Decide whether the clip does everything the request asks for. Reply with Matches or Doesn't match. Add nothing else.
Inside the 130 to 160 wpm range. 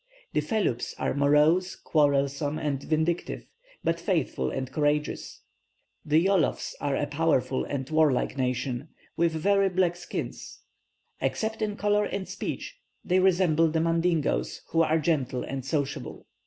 Matches